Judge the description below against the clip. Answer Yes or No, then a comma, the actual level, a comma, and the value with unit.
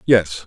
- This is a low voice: Yes, low, 100 Hz